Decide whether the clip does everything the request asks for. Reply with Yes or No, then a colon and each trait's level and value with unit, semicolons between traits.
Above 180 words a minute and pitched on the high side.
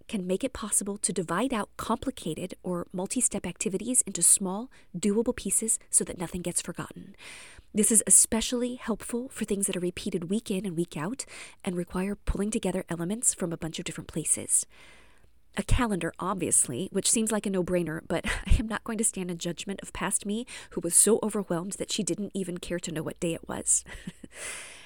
Yes: average, 200 wpm; high, 195 Hz